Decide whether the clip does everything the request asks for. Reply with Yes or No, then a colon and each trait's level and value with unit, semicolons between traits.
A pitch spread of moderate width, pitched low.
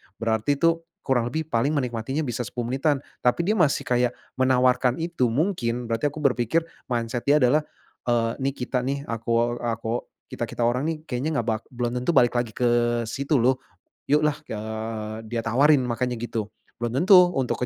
Yes: average, 3.3 semitones; low, 125 Hz